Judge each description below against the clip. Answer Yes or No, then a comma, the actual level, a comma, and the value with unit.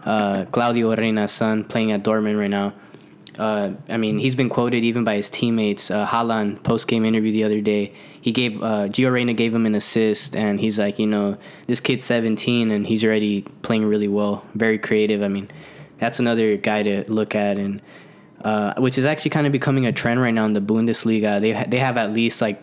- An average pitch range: No, narrow, 2.1 semitones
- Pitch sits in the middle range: No, low, 110 Hz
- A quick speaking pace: Yes, fast, 215 wpm